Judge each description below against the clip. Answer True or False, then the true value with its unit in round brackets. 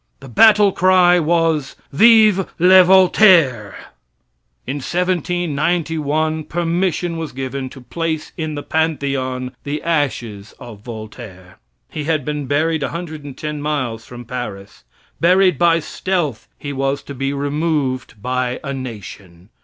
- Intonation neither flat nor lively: True (4.7 semitones)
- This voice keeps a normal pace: False (120 wpm)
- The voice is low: False (150 Hz)